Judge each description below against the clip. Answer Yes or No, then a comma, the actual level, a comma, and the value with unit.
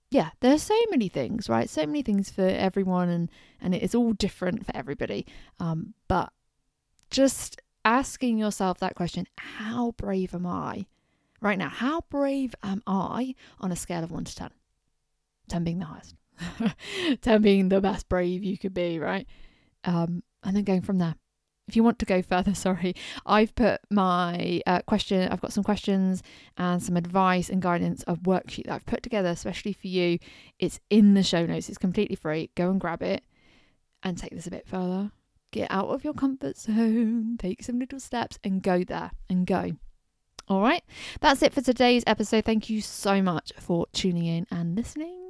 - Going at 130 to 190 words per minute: Yes, average, 185 wpm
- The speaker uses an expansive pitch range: No, average, 4.1 semitones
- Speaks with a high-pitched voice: Yes, high, 195 Hz